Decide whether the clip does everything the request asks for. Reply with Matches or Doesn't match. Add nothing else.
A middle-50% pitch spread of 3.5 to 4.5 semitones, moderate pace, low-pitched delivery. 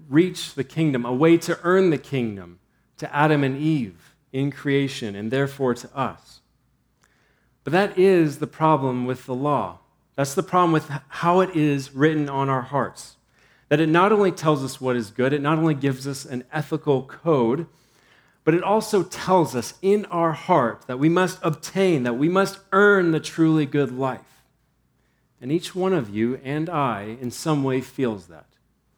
Doesn't match